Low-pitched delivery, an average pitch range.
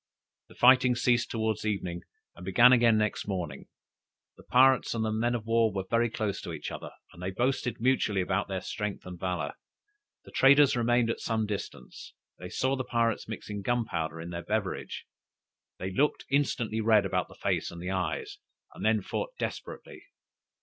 Yes: low, 110 Hz; average, 4.3 semitones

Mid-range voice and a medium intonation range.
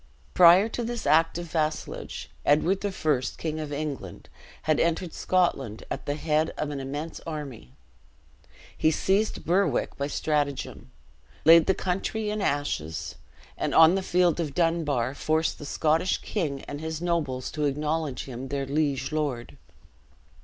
Yes: medium, 155 Hz; average, 3.2 semitones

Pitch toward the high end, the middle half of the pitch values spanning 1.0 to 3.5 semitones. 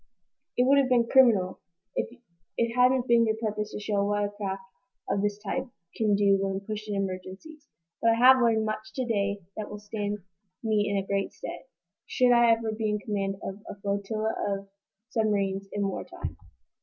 Yes: high, 210 Hz; narrow, 2.5 semitones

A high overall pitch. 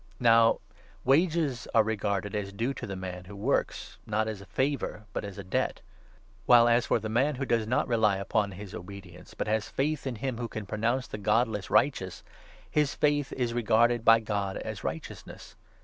No: low, 110 Hz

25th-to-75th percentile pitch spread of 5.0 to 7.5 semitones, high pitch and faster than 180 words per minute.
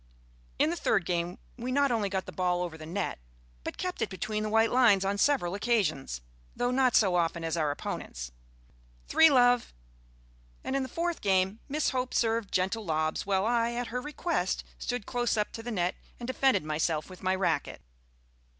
Yes: wide, 5.5 semitones; high, 210 Hz; average, 190 wpm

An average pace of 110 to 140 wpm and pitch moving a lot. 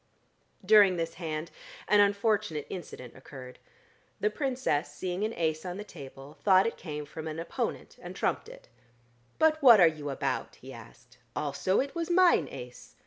No: average, 165 wpm; wide, 6.7 semitones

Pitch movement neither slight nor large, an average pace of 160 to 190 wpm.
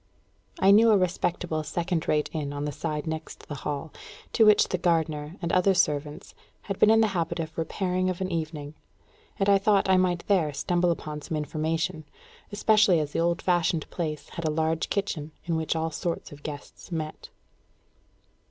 Yes: average, 3.1 semitones; average, 185 wpm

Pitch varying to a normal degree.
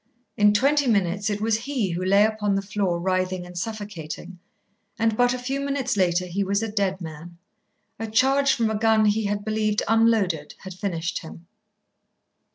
Yes: average, 3.4 semitones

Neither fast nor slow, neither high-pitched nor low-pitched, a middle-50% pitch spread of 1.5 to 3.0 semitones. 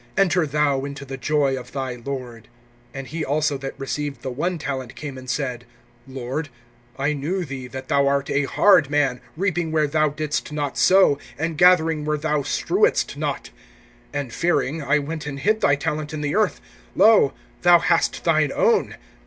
Yes: average, 175 wpm; medium, 145 Hz; narrow, 2.6 semitones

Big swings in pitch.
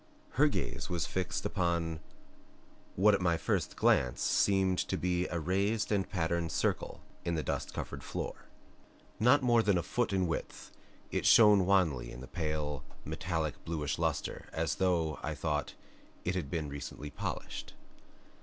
No: average, 3.6 semitones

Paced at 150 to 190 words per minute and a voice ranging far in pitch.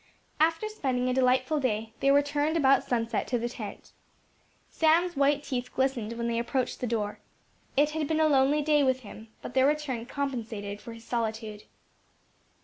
No: average, 170 wpm; average, 3.9 semitones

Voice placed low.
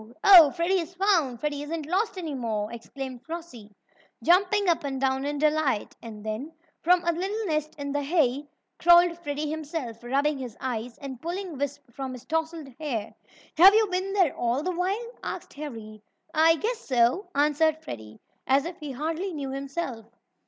No: very high, 300 Hz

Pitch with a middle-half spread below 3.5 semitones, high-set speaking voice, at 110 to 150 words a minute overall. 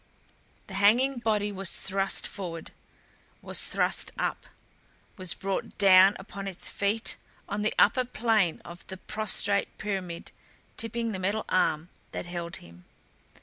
Yes: average, 2.7 semitones; high, 195 Hz; slow, 135 wpm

